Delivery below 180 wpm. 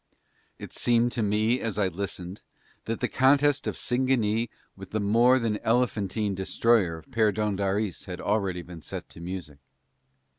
Yes: average, 150 wpm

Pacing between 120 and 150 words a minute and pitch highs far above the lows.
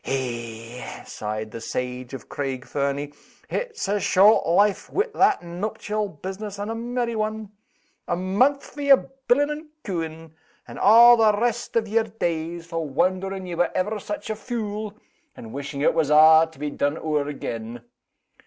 No: average, 165 wpm; wide, 7.2 semitones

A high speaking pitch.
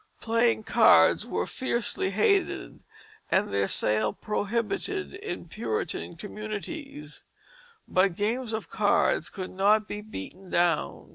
Yes: high, 210 Hz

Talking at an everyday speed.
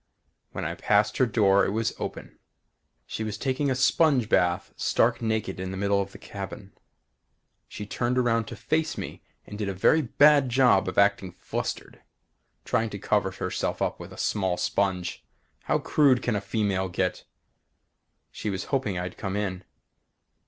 Yes: average, 170 wpm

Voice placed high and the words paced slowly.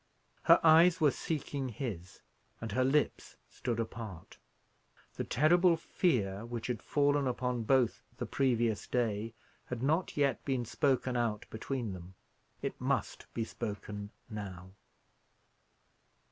No: low, 120 Hz; slow, 125 wpm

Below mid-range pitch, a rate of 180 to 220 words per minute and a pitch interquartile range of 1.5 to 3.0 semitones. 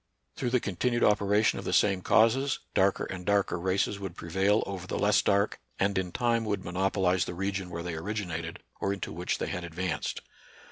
Yes: very low, 95 Hz; average, 190 wpm; narrow, 2.5 semitones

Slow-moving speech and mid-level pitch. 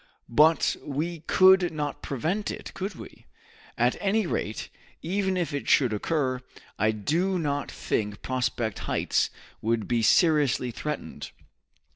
Yes: slow, 130 wpm; medium, 150 Hz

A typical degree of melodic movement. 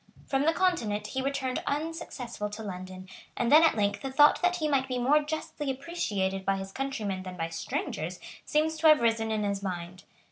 No: wide, 7.2 semitones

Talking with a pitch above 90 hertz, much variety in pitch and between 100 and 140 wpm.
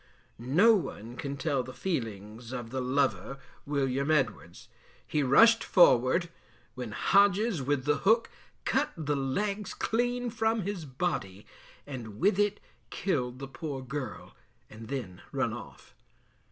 Yes: medium, 140 Hz; wide, 7.4 semitones; slow, 135 wpm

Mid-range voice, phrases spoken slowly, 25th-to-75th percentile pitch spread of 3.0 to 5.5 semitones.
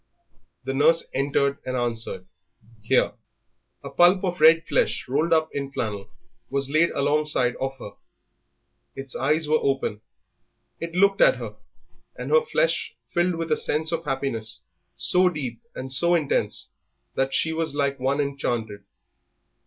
No: medium, 145 Hz; average, 145 wpm; average, 3.8 semitones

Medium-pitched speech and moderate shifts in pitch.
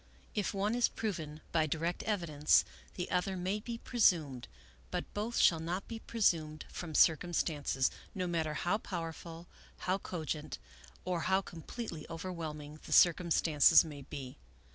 Yes: medium, 170 Hz; average, 3.5 semitones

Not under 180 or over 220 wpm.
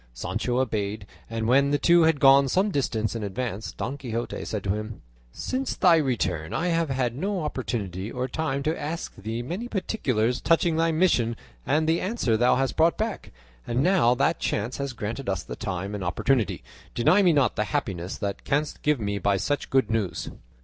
Yes: average, 190 wpm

